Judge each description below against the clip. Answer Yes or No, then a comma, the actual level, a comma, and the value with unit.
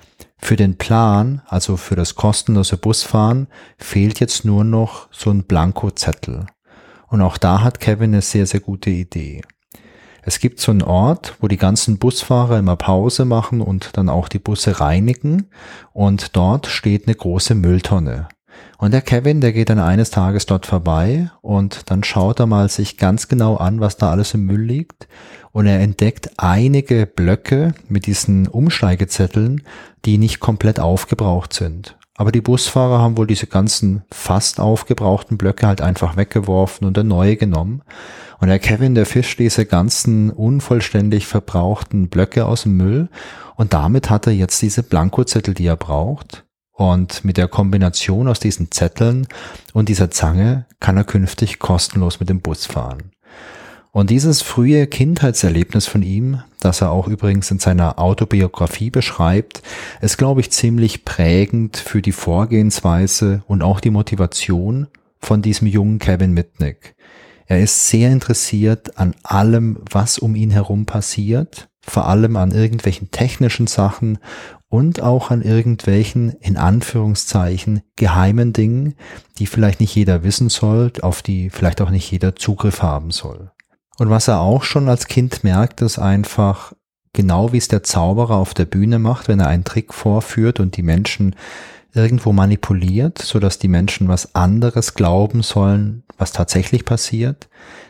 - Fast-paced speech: No, average, 155 wpm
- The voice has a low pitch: Yes, low, 105 Hz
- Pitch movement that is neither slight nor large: Yes, average, 3.4 semitones